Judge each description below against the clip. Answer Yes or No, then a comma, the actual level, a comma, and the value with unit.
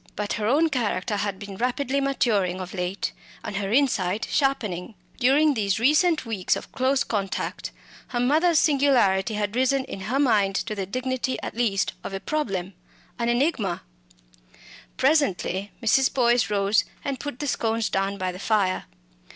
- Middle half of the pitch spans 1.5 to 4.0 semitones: No, wide, 5.5 semitones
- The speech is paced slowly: No, average, 160 wpm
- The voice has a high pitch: Yes, high, 230 Hz